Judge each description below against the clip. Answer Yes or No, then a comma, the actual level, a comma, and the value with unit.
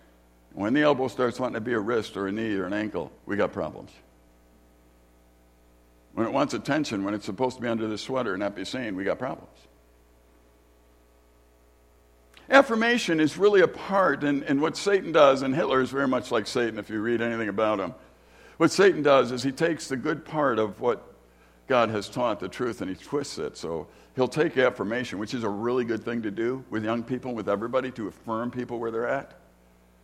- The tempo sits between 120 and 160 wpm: No, fast, 205 wpm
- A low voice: Yes, low, 115 Hz